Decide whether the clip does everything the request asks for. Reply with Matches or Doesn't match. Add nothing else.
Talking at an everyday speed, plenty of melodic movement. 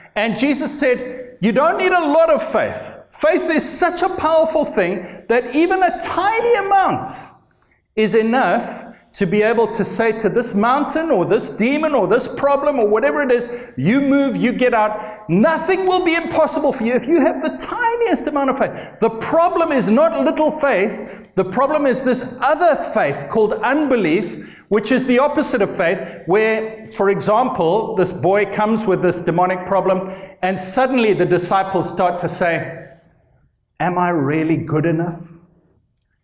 Matches